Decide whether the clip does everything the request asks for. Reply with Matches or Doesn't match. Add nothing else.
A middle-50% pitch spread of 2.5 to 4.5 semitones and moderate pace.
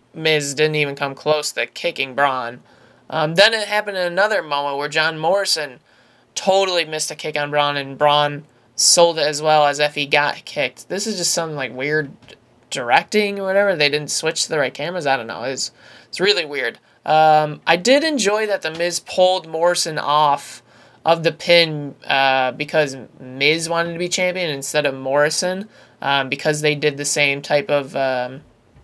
Matches